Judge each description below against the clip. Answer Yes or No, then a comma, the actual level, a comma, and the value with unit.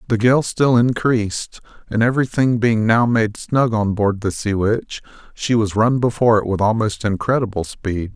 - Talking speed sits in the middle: Yes, average, 175 wpm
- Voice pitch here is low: Yes, low, 110 Hz